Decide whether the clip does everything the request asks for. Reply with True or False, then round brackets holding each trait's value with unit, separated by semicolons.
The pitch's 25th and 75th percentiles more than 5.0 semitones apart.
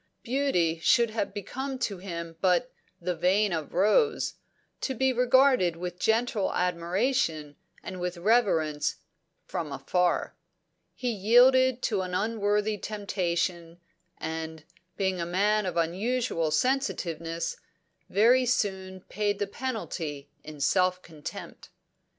True (5.5 semitones)